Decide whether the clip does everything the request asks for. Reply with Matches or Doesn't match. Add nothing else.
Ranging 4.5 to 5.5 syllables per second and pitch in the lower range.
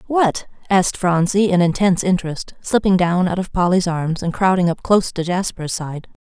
Doesn't match